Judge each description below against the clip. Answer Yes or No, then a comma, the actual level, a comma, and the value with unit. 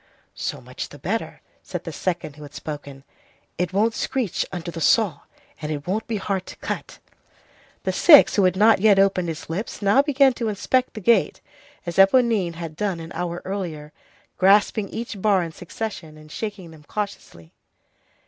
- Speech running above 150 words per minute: Yes, average, 175 wpm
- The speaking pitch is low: No, high, 190 Hz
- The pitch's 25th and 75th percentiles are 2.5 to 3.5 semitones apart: No, average, 4.7 semitones